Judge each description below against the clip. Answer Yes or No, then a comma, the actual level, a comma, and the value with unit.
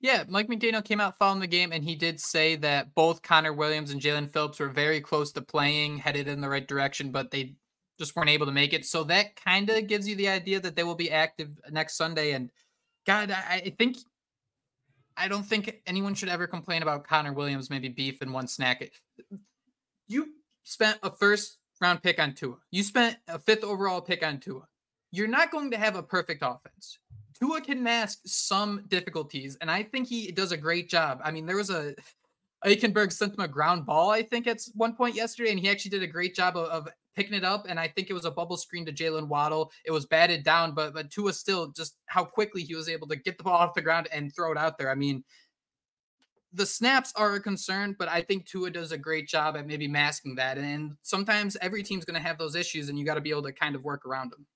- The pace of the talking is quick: Yes, fast, 235 wpm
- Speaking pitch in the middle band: Yes, medium, 170 Hz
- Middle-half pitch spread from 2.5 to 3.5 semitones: No, average, 4.9 semitones